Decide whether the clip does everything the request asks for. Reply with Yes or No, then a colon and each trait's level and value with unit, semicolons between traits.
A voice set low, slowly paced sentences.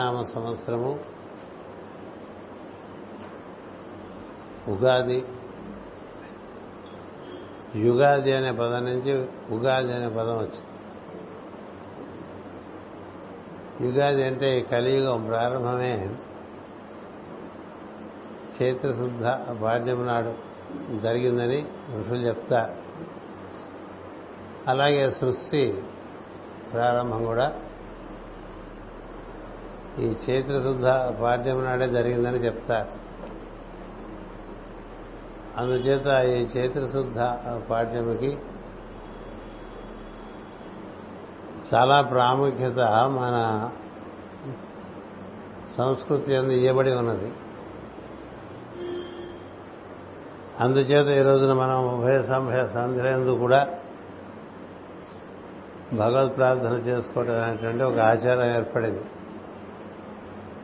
Yes: low, 125 Hz; slow, 55 wpm